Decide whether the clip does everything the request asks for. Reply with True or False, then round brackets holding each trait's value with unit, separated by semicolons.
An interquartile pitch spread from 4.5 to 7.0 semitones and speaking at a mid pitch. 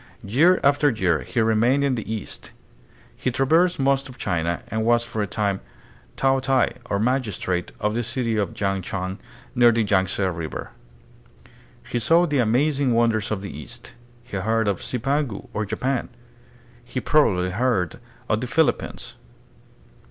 False (4.9 semitones; 115 Hz)